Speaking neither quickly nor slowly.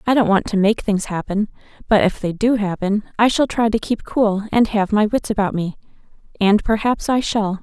No: fast, 220 wpm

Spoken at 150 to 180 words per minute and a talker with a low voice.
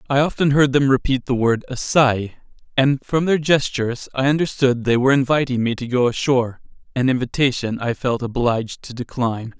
Yes: average, 175 wpm; low, 130 Hz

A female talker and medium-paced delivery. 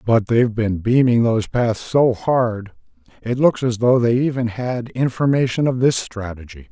No: male; average, 170 wpm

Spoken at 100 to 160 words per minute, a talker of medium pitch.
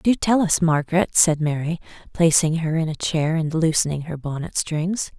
No: average, 185 wpm; medium, 160 Hz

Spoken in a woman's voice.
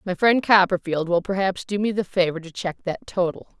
Yes: female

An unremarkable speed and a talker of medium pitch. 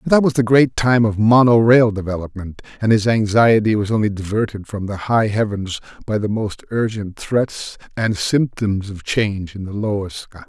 No: average, 190 wpm; low, 105 Hz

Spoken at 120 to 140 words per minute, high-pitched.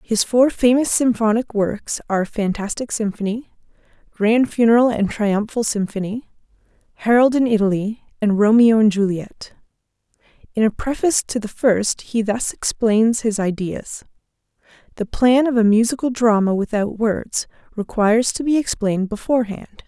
Yes: slow, 135 wpm; high, 220 Hz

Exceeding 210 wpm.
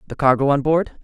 Yes: fast, 230 wpm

